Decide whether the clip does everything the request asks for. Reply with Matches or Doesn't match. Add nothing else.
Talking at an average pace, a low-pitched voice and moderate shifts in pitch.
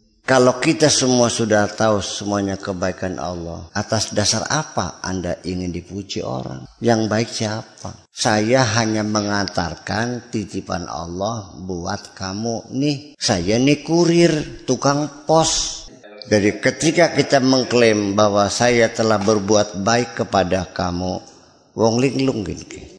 Matches